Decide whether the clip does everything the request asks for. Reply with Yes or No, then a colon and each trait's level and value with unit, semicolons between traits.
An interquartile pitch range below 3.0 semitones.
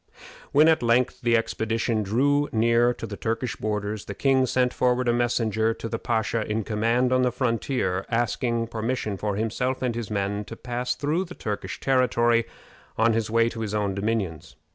Yes: narrow, 2.5 semitones